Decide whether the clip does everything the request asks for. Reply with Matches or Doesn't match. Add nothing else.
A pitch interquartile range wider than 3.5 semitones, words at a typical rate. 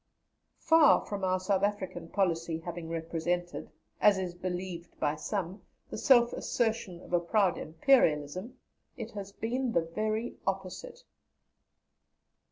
Doesn't match